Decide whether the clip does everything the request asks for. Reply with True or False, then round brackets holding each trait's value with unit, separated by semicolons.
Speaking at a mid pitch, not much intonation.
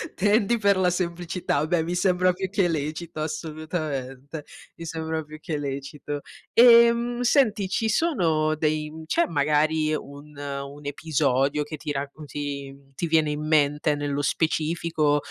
False (155 Hz; 3.4 semitones)